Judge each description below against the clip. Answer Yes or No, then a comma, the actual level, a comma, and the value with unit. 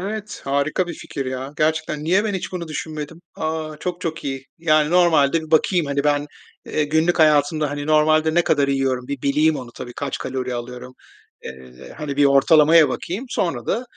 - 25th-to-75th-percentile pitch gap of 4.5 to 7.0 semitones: No, average, 2.8 semitones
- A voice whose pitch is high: No, medium, 150 Hz